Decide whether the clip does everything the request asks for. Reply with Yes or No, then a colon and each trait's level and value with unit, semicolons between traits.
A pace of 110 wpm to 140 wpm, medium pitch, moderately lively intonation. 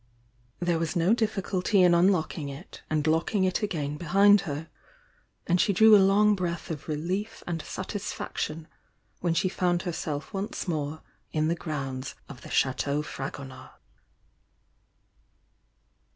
Yes: slow, 135 wpm; medium, 170 Hz; average, 4.1 semitones